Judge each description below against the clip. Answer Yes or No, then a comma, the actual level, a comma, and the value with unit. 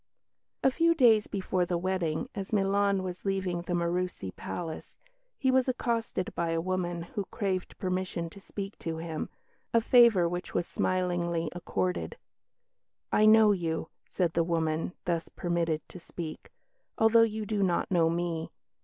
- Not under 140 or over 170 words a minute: Yes, average, 155 wpm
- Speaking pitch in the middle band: Yes, medium, 180 Hz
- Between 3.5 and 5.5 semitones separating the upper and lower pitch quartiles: No, average, 3.1 semitones